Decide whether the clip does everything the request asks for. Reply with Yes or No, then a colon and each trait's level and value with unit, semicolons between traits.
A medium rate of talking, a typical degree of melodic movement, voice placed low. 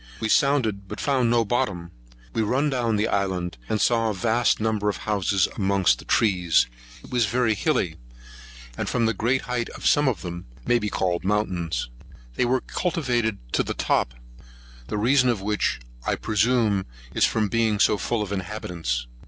Yes: average, 180 wpm; average, 3.9 semitones; low, 110 Hz